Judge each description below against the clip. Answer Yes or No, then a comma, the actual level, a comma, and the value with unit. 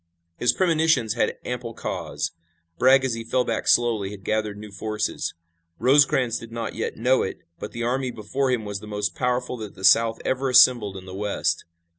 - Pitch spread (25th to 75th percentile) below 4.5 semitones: Yes, average, 3.2 semitones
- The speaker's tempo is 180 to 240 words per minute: Yes, average, 190 wpm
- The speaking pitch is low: Yes, low, 115 Hz